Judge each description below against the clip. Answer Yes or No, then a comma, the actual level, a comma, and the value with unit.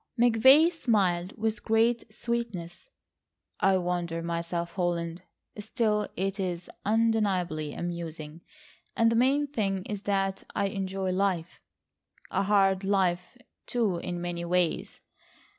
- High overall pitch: Yes, high, 195 Hz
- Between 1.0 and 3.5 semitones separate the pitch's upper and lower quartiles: No, average, 4.1 semitones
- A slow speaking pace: Yes, slow, 110 wpm